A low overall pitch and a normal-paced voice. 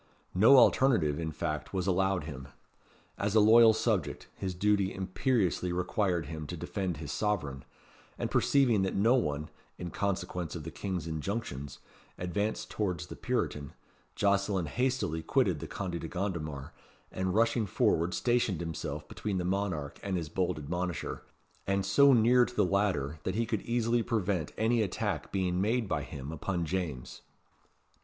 Yes: very low, 95 Hz; average, 155 wpm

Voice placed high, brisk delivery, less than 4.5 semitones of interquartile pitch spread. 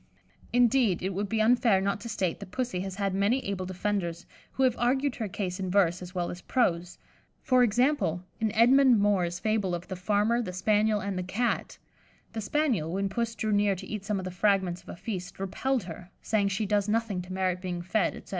Yes: high, 200 Hz; fast, 215 wpm; average, 3.6 semitones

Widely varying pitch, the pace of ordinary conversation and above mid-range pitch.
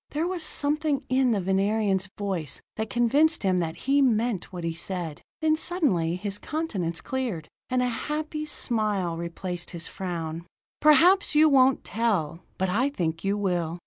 Yes: wide, 8.1 semitones; average, 160 wpm; high, 210 Hz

